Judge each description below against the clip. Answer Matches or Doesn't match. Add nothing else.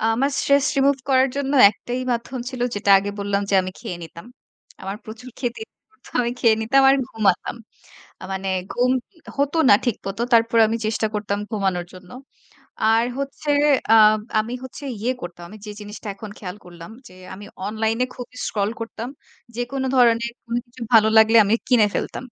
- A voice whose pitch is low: Doesn't match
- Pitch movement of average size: Matches